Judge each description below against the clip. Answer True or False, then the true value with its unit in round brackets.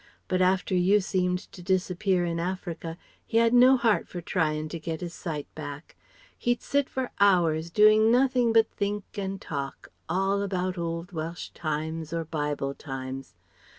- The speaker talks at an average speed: True (160 wpm)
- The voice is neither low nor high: True (180 Hz)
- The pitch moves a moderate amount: True (4.0 semitones)